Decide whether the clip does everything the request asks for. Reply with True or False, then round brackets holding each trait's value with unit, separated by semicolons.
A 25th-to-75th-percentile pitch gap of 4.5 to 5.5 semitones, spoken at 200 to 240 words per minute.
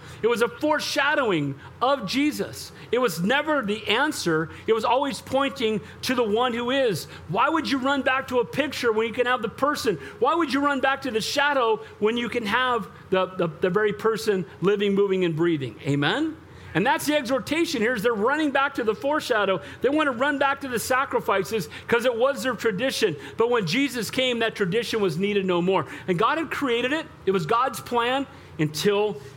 True (5.2 semitones; 205 wpm)